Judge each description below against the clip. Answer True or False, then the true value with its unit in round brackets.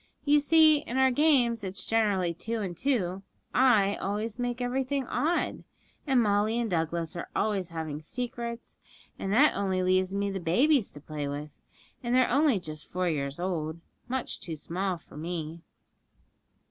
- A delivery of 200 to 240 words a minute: False (160 wpm)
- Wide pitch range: True (6.4 semitones)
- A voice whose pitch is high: True (200 Hz)